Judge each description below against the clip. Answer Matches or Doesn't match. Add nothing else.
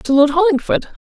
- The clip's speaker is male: Doesn't match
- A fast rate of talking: Doesn't match